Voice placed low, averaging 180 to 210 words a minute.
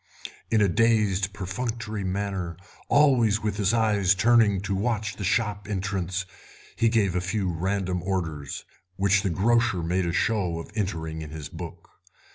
No: low, 100 Hz; average, 155 wpm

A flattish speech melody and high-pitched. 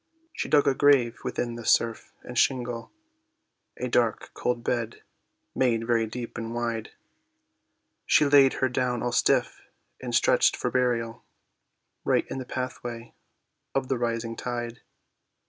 No: narrow, 1.6 semitones; low, 120 Hz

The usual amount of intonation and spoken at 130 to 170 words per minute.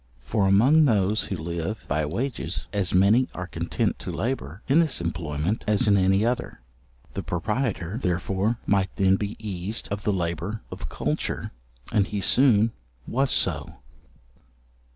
Yes: average, 3.5 semitones; average, 150 wpm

